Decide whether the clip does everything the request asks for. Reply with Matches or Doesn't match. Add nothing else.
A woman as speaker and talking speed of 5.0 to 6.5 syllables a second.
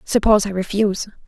Doesn't match